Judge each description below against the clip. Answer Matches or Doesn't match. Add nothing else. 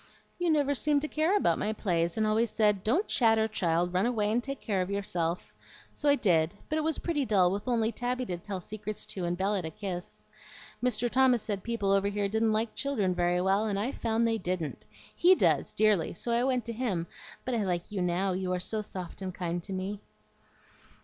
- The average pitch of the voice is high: Matches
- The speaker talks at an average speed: Doesn't match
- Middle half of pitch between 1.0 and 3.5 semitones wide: Doesn't match